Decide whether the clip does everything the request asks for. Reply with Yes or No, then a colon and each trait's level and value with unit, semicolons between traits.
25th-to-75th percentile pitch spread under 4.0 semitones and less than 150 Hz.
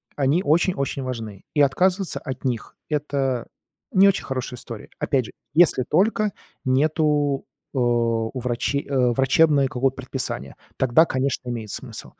Yes: average, 3.3 semitones; low, 135 Hz